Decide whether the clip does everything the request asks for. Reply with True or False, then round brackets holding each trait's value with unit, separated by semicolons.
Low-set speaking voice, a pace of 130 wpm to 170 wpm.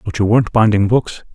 False (110 Hz; 225 wpm)